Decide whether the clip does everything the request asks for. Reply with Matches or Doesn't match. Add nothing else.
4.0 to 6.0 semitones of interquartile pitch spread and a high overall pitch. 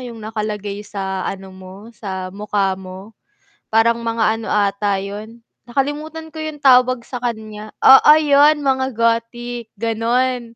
Doesn't match